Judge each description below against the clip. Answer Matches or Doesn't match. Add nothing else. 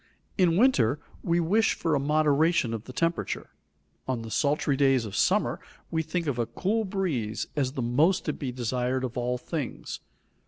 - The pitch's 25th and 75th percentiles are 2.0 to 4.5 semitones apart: Doesn't match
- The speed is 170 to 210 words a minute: Matches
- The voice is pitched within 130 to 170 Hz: Matches